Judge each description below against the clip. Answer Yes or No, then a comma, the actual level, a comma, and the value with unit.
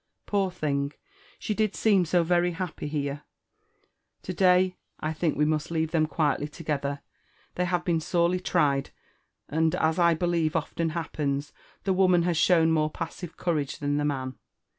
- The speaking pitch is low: No, medium, 165 Hz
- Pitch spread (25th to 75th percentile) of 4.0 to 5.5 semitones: No, average, 2.9 semitones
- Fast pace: No, average, 160 wpm